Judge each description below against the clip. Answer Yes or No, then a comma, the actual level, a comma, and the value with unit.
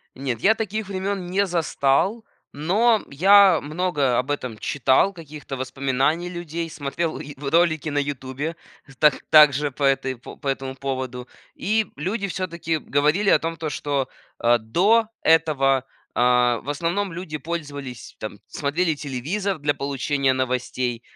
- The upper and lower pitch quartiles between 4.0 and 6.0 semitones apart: Yes, average, 4.6 semitones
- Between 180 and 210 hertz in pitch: No, medium, 150 Hz